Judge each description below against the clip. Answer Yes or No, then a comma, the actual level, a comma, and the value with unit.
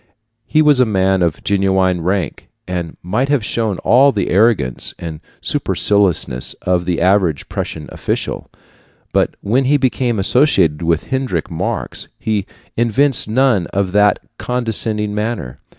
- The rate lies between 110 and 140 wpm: Yes, slow, 135 wpm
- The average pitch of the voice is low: Yes, low, 100 Hz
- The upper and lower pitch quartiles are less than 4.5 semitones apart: No, average, 4.9 semitones